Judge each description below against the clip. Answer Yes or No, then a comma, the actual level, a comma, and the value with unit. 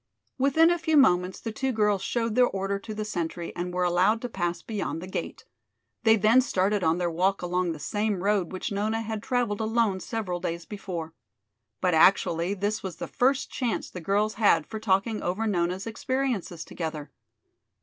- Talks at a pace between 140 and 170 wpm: No, average, 185 wpm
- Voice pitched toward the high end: Yes, high, 200 Hz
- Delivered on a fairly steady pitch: No, average, 3.8 semitones